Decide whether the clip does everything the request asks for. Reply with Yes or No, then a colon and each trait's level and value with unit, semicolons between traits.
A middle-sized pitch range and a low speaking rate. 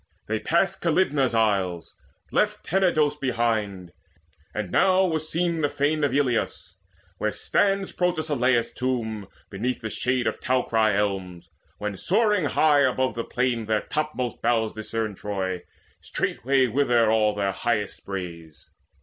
No: wide, 6.1 semitones; slow, 130 wpm